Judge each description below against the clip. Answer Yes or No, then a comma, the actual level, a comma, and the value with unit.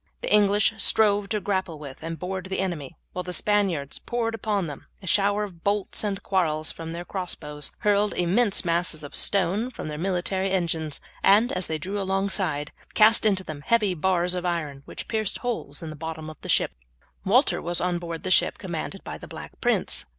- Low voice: No, medium, 185 Hz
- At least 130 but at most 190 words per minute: No, average, 200 wpm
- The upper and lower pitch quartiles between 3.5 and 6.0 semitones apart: Yes, average, 3.8 semitones